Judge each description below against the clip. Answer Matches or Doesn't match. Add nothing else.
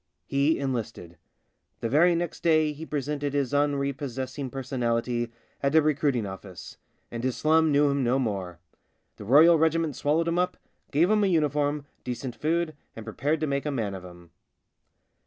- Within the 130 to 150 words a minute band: Doesn't match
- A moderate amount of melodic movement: Matches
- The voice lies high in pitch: Doesn't match